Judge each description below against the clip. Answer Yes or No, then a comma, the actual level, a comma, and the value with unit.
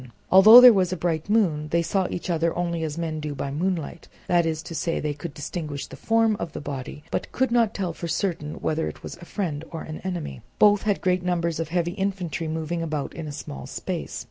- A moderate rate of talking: No, fast, 230 wpm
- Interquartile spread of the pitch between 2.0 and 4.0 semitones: Yes, average, 3.1 semitones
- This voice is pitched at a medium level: Yes, medium, 170 Hz